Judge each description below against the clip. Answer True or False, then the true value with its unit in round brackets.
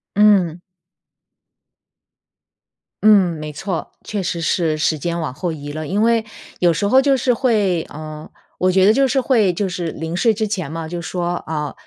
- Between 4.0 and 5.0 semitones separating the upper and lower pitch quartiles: True (4.7 semitones)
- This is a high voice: False (180 Hz)